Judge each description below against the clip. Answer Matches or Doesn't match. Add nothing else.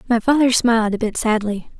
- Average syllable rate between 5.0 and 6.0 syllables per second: Matches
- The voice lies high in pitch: Matches